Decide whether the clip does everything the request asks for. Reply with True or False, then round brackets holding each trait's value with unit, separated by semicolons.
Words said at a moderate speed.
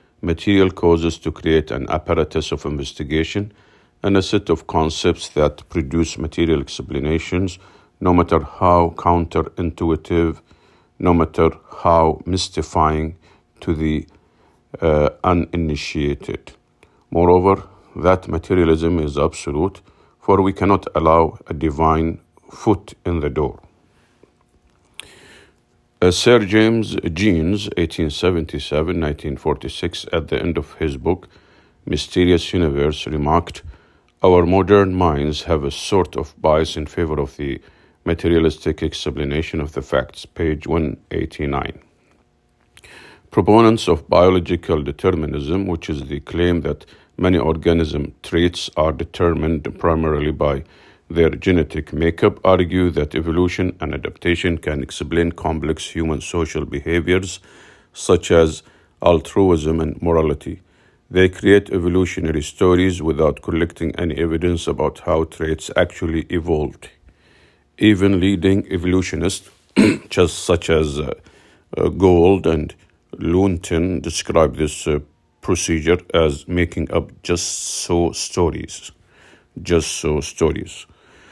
False (110 wpm)